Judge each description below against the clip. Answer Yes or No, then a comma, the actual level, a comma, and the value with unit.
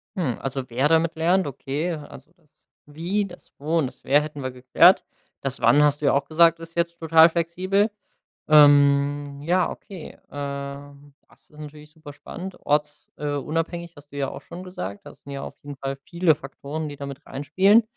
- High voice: No, medium, 150 Hz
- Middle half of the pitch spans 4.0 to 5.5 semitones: No, average, 3.1 semitones